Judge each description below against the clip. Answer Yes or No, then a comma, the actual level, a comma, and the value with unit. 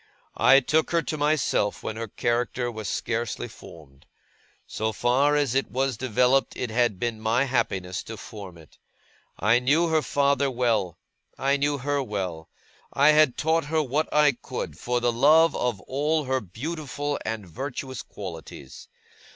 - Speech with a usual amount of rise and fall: Yes, average, 4.6 semitones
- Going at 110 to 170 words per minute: Yes, average, 160 wpm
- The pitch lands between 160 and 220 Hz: No, low, 125 Hz